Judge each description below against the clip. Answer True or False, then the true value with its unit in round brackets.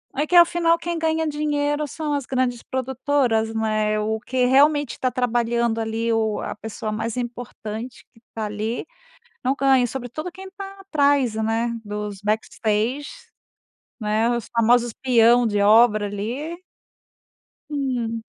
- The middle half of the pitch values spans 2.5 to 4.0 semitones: False (4.5 semitones)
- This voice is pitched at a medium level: False (240 Hz)